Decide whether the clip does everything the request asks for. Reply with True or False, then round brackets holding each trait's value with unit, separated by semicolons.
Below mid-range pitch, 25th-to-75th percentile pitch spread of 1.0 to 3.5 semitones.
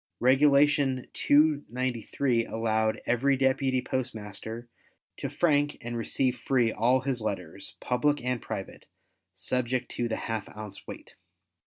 True (125 Hz; 3.2 semitones)